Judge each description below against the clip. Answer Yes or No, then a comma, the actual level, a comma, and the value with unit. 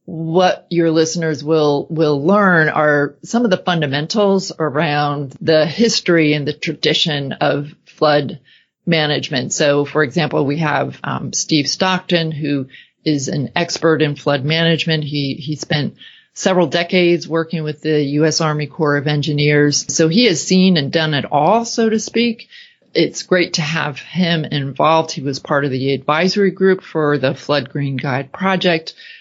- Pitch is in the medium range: Yes, medium, 160 Hz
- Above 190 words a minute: No, average, 160 wpm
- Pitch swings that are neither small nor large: Yes, average, 3.3 semitones